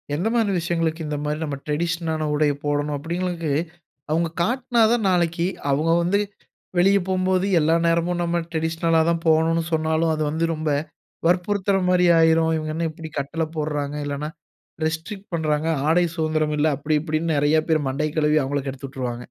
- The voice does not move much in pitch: Yes, narrow, 2.2 semitones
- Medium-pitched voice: Yes, medium, 160 Hz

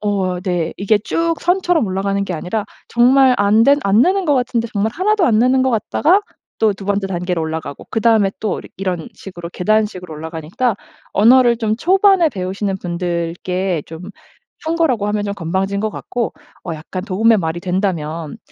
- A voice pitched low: No, high, 200 Hz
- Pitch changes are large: No, average, 5.0 semitones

